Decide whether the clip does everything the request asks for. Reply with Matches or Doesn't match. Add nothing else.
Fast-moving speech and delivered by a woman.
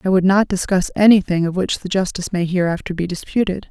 Matches